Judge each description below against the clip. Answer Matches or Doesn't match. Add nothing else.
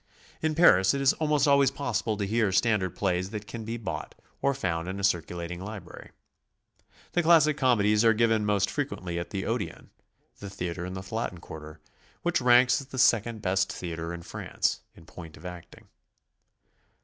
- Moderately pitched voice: Doesn't match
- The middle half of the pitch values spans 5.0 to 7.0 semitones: Matches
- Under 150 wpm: Doesn't match